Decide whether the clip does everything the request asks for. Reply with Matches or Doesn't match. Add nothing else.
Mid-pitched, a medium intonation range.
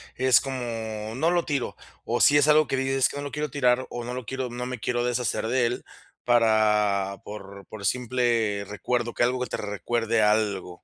Doesn't match